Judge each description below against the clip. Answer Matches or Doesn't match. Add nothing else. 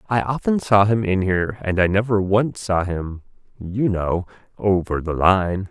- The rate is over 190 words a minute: Doesn't match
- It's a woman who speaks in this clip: Doesn't match